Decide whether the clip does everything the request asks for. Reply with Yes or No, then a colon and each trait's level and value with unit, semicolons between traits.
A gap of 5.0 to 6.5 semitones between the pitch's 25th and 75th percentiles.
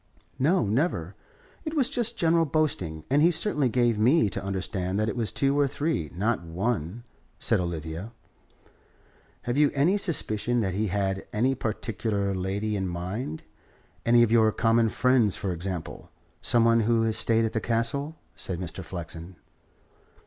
Yes: wide, 5.4 semitones